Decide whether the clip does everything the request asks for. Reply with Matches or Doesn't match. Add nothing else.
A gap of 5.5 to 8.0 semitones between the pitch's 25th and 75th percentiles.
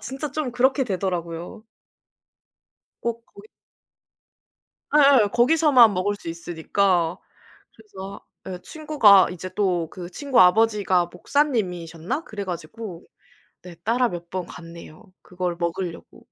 Doesn't match